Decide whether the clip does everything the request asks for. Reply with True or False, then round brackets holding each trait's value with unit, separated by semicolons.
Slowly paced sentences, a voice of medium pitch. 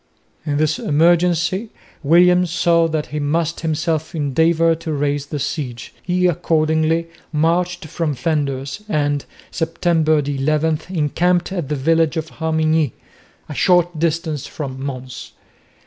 True (125 wpm; 160 Hz)